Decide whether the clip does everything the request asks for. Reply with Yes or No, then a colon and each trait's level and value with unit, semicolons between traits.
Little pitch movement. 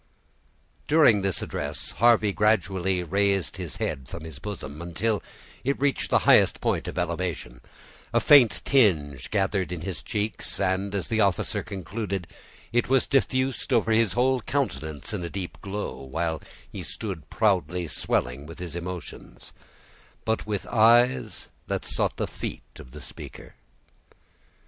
No: average, 4.6 semitones